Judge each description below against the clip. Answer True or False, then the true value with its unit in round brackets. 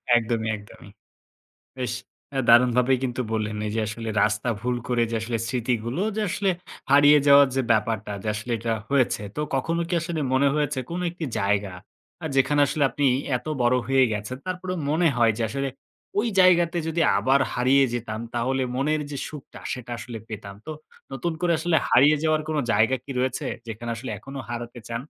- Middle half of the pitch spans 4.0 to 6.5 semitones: True (4.3 semitones)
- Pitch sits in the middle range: False (125 Hz)